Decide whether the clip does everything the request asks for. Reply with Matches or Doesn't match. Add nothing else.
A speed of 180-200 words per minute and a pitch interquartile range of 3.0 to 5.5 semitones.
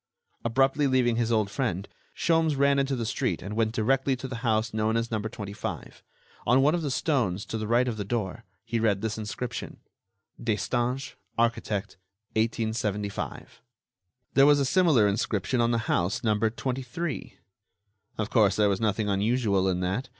Doesn't match